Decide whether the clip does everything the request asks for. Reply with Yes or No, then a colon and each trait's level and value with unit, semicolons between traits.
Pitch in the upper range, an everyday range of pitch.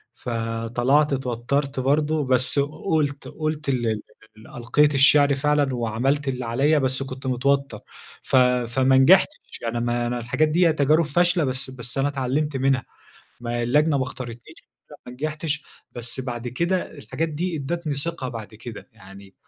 No: low, 135 Hz; average, 3.5 semitones